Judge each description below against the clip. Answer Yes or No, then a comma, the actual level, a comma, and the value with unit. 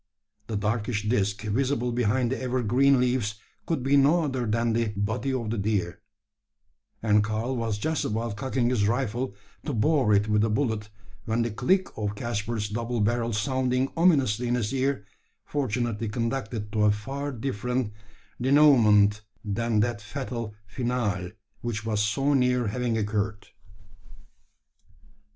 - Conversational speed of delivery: Yes, average, 145 wpm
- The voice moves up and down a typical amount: Yes, average, 3.5 semitones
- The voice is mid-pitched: No, low, 115 Hz